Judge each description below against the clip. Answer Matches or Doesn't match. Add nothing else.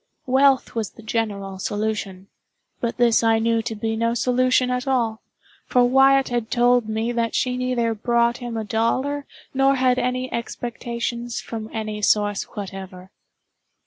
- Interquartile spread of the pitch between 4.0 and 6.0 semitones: Doesn't match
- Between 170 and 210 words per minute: Doesn't match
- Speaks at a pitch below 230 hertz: Doesn't match